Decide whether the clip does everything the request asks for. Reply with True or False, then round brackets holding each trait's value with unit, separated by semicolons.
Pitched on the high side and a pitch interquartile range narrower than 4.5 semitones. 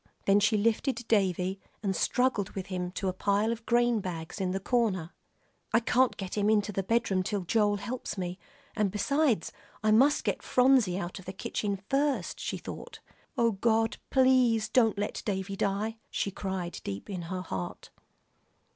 True (205 Hz; 3.5 semitones)